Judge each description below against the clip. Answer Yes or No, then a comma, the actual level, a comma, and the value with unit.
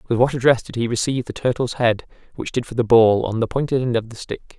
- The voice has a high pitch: No, low, 120 Hz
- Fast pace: Yes, fast, 275 wpm